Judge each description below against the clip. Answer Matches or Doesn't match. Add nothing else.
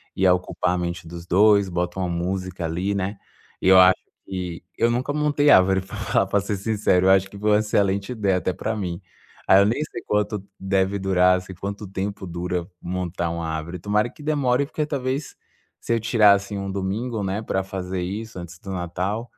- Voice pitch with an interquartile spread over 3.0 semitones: Doesn't match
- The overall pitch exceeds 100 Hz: Doesn't match